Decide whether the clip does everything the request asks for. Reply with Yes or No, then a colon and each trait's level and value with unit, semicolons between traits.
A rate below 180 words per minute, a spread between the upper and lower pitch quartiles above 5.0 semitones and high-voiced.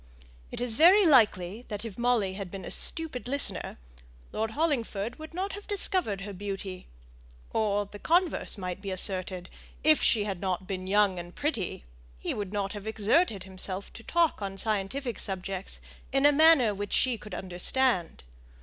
Yes: average, 170 wpm; wide, 5.6 semitones; high, 210 Hz